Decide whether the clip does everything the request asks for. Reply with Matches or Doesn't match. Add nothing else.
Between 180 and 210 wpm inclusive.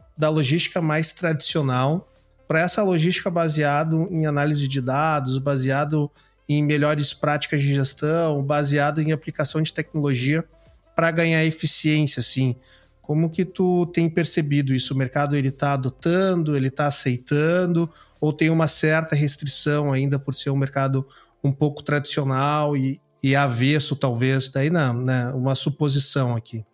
Doesn't match